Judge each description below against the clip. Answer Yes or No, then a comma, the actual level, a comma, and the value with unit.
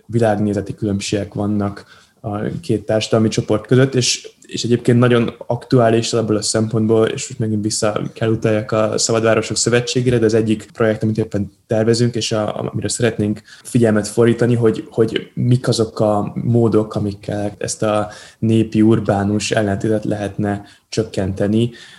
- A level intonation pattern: Yes, narrow, 1.7 semitones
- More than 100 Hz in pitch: Yes, low, 110 Hz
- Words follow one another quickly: No, average, 140 wpm